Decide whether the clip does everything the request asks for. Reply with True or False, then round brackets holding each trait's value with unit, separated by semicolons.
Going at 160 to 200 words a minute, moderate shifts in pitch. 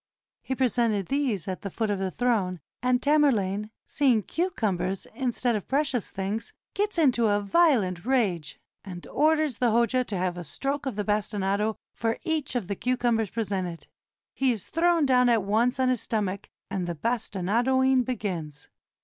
True (170 wpm; 4.9 semitones)